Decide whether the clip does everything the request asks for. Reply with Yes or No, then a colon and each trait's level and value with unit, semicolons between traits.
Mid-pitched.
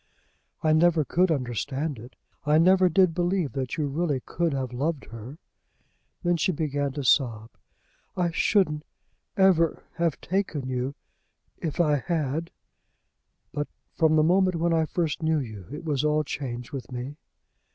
Yes: medium, 155 Hz